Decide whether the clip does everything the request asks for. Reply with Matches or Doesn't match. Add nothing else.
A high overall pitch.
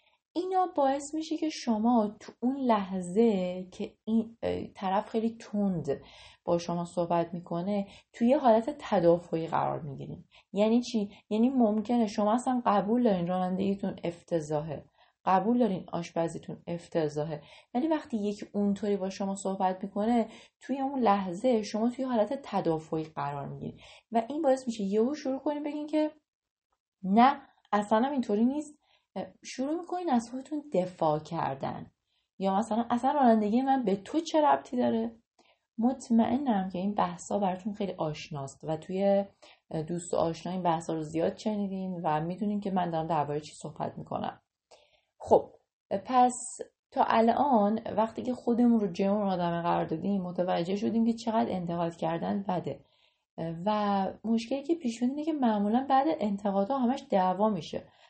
Matches